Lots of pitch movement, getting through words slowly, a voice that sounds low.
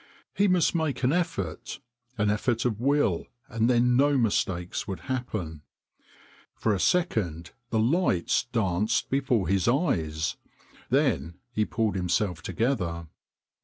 Yes: wide, 6.6 semitones; slow, 130 wpm; low, 110 Hz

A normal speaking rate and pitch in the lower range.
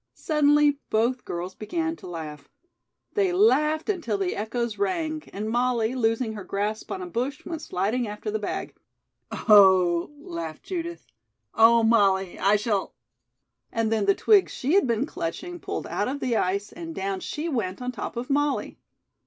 No: average, 170 wpm; high, 235 Hz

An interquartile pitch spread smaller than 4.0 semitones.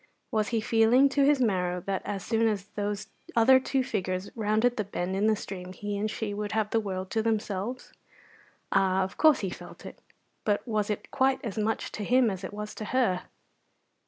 Yes: average, 2.7 semitones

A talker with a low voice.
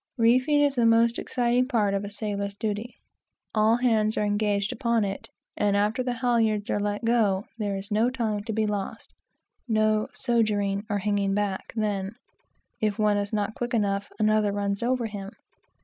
No: high, 215 Hz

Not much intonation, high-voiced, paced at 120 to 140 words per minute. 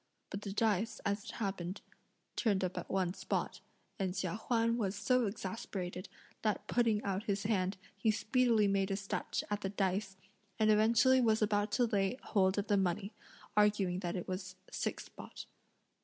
No: narrow, 2.3 semitones; high, 205 Hz; average, 170 wpm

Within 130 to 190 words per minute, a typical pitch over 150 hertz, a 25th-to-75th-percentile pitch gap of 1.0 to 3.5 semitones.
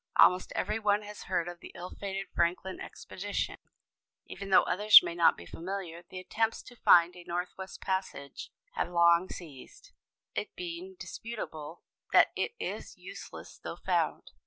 Yes: average, 155 wpm; medium, 185 Hz; average, 3.2 semitones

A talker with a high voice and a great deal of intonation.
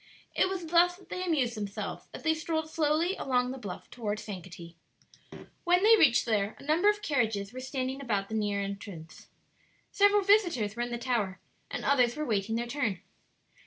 Yes: very high, 250 Hz; wide, 7.6 semitones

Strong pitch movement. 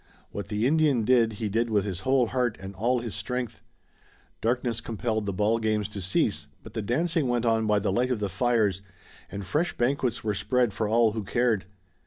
No: average, 3.0 semitones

